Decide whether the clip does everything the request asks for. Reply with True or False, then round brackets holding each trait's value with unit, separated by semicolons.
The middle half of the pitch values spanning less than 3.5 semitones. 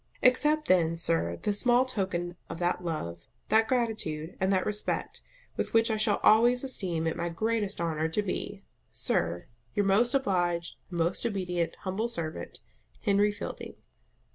False (4.7 semitones)